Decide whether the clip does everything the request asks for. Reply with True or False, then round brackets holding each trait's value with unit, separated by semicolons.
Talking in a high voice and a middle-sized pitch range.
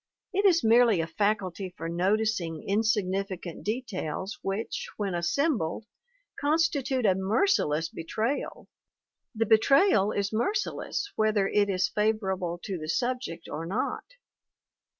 True (210 Hz; 4.5 semitones)